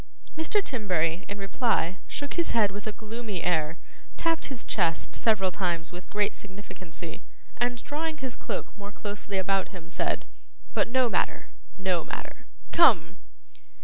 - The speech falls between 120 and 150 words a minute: Yes, average, 145 wpm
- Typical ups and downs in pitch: Yes, average, 4.7 semitones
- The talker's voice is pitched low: No, high, 205 Hz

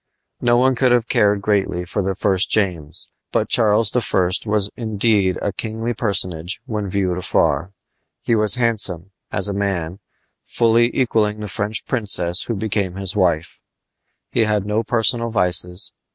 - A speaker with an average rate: Yes, average, 150 wpm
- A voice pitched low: Yes, low, 105 Hz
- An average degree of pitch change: Yes, average, 3.2 semitones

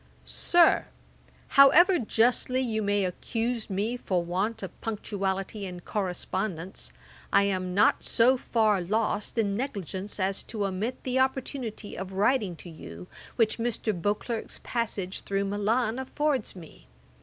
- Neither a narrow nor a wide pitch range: Yes, average, 3.8 semitones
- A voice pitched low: No, high, 210 Hz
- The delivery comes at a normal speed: No, slow, 130 wpm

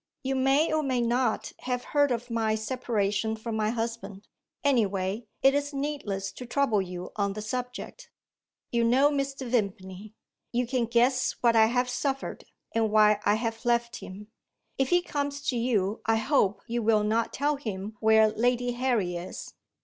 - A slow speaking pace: No, average, 170 wpm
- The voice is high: Yes, high, 235 Hz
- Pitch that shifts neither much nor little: Yes, average, 3.3 semitones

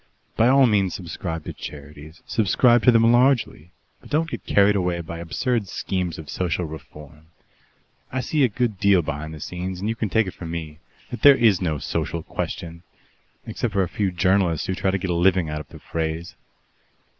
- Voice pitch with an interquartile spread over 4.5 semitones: Yes, average, 5.2 semitones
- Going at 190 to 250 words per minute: Yes, average, 200 wpm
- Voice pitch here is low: Yes, very low, 90 Hz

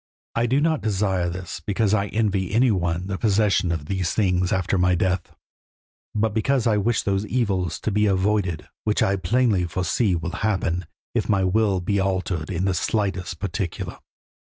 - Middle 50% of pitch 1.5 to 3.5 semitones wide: Yes, average, 2.8 semitones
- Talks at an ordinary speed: Yes, average, 175 wpm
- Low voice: Yes, very low, 95 Hz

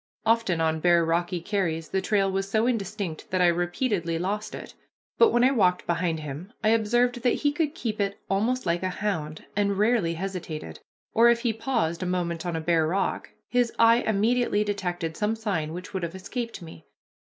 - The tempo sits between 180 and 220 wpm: Yes, average, 195 wpm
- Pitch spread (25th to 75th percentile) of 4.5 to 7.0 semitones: Yes, average, 4.8 semitones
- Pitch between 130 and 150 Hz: No, high, 195 Hz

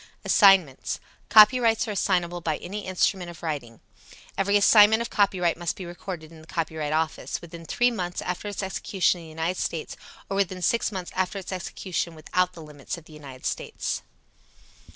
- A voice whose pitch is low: No, medium, 180 Hz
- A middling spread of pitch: Yes, average, 3.4 semitones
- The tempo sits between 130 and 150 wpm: No, average, 175 wpm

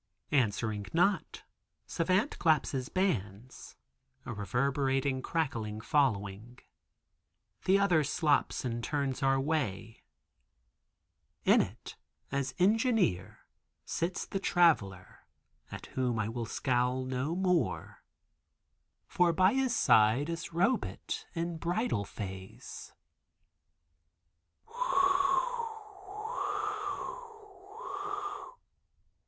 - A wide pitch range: Yes, wide, 7.3 semitones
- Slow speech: Yes, slow, 80 wpm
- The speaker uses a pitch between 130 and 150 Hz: Yes, low, 135 Hz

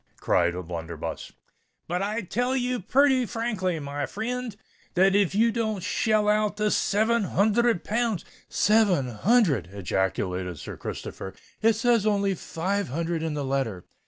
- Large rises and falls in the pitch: Yes, wide, 7.7 semitones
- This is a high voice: Yes, high, 200 Hz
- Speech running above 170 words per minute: No, average, 140 wpm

